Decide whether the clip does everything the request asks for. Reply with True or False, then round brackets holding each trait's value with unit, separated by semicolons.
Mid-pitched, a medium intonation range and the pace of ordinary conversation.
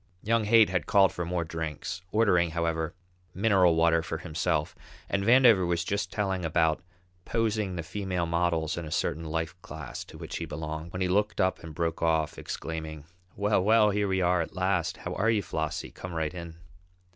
False (85 Hz; 3.2 semitones; 190 wpm)